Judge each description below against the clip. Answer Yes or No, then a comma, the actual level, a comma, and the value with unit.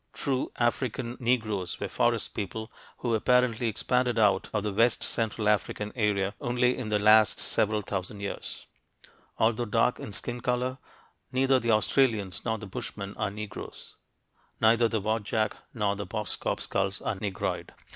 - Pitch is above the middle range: No, low, 110 Hz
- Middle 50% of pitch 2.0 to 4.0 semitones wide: Yes, average, 2.8 semitones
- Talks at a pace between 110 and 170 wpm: Yes, average, 150 wpm